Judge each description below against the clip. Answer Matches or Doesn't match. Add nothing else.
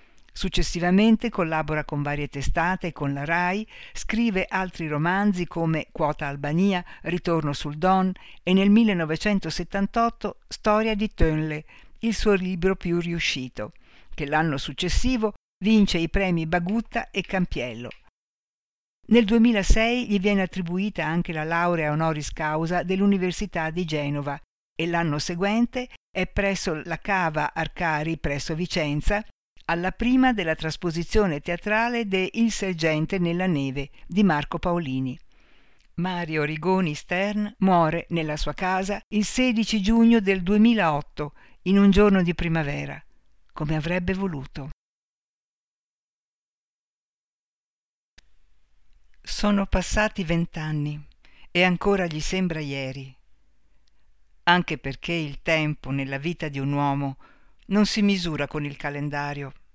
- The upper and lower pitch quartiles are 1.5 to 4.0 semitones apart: Doesn't match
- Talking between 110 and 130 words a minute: Matches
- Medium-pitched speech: Matches